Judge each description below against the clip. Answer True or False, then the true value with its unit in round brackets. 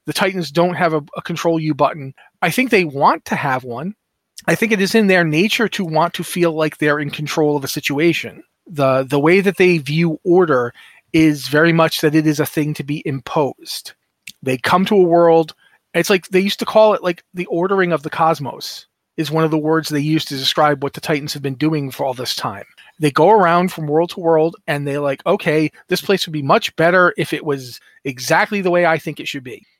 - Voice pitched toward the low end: False (160 Hz)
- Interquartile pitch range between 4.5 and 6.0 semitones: False (3.2 semitones)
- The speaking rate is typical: False (235 wpm)